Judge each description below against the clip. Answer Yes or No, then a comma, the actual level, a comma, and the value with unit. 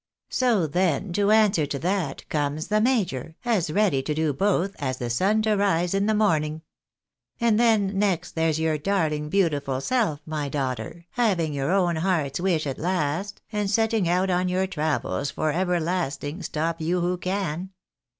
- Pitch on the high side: No, medium, 175 Hz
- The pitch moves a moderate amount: Yes, average, 4.7 semitones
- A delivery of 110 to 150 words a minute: No, average, 170 wpm